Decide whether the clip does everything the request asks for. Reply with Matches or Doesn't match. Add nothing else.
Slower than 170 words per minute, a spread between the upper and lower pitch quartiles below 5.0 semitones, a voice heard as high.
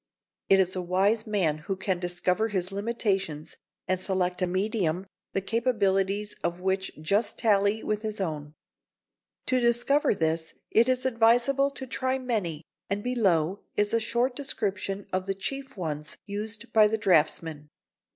Matches